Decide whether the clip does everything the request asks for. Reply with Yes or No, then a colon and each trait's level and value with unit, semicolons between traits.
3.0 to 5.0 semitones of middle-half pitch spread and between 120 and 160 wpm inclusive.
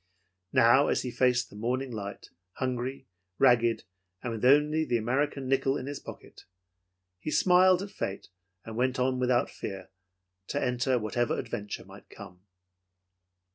No: narrow, 2.5 semitones; average, 145 wpm